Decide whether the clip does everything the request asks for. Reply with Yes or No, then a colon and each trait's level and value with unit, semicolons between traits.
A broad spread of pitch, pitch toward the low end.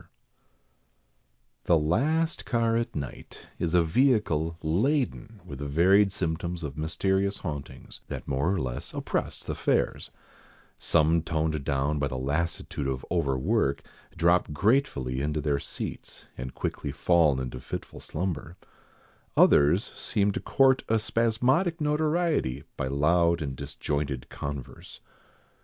Yes: wide, 6.5 semitones; very low, 80 Hz